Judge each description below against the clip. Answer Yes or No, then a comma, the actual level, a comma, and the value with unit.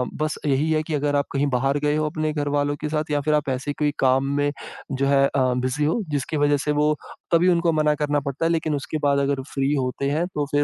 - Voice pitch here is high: No, medium, 145 Hz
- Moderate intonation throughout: No, narrow, 1.7 semitones